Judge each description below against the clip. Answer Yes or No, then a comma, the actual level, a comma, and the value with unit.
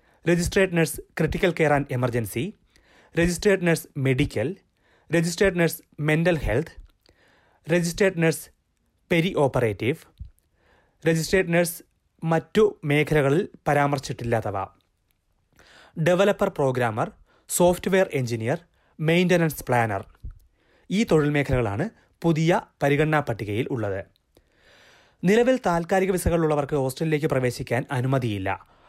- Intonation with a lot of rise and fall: Yes, wide, 6.4 semitones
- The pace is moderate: Yes, average, 85 wpm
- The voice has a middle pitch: Yes, medium, 150 Hz